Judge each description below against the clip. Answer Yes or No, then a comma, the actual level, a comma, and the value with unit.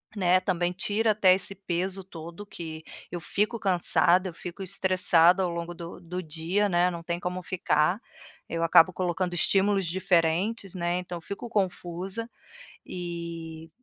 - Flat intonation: Yes, narrow, 2.1 semitones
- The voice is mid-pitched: Yes, medium, 180 Hz